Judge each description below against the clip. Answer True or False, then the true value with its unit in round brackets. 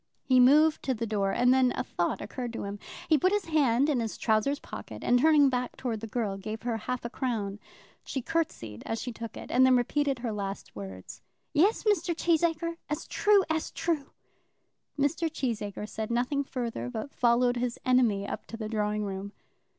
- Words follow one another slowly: False (195 wpm)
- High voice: True (245 Hz)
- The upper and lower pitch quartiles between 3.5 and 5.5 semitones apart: True (5.1 semitones)